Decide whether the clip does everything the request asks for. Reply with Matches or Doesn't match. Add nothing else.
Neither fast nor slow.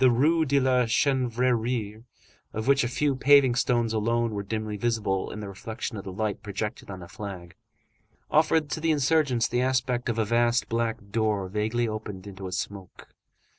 Matches